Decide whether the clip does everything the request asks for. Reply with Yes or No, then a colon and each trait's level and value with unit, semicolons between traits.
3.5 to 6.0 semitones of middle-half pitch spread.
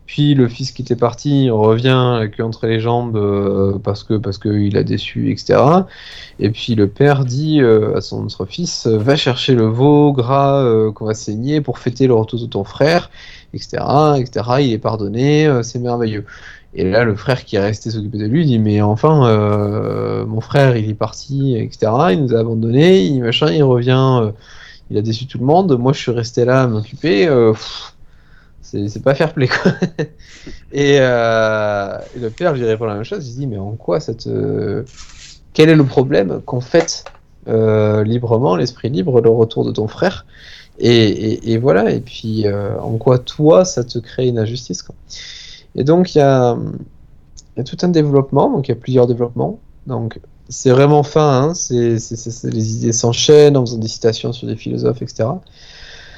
Yes: average, 3.9 semitones